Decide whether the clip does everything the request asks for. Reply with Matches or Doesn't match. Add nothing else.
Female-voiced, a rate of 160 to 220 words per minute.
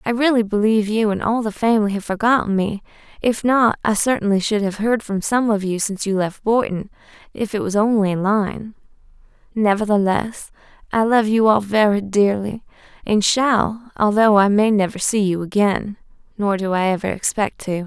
Matches